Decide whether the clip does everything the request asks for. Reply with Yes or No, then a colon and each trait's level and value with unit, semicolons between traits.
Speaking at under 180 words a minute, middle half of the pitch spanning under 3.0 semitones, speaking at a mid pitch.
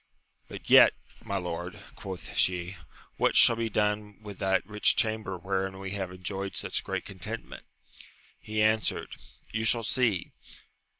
No: average, 140 wpm; narrow, 2.4 semitones; low, 100 Hz